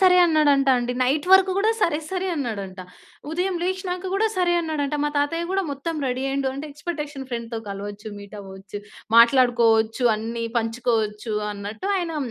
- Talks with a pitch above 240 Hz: Yes, very high, 270 Hz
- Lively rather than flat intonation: Yes, wide, 6.8 semitones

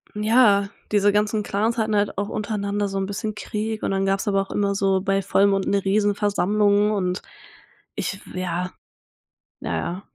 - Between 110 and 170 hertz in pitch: No, high, 200 Hz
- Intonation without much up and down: Yes, narrow, 1.3 semitones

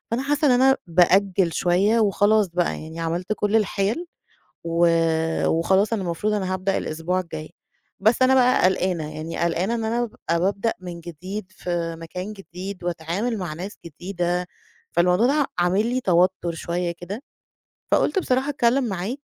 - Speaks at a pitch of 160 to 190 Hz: Yes, medium, 185 Hz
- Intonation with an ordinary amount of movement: Yes, average, 4.1 semitones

